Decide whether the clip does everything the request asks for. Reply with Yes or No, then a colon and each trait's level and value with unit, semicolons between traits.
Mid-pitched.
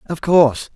Yes: medium, 150 Hz